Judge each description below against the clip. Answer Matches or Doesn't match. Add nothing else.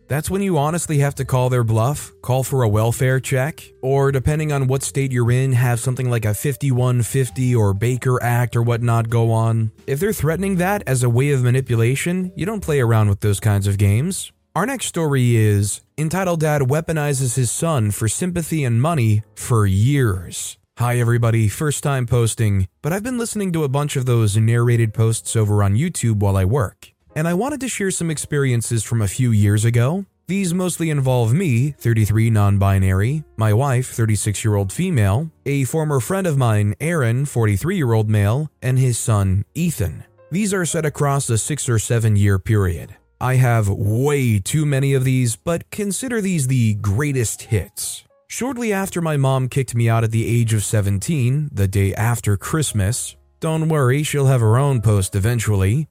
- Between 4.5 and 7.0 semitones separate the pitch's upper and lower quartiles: Matches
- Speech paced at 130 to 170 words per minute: Doesn't match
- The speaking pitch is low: Matches